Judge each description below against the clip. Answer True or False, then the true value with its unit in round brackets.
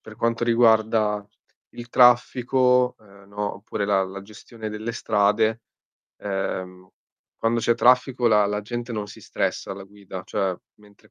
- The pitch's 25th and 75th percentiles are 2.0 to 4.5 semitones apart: True (2.7 semitones)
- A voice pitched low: True (110 Hz)